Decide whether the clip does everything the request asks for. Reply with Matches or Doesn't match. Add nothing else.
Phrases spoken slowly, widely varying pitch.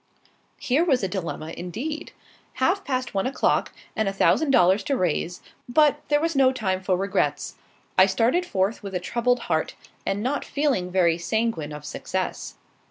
Doesn't match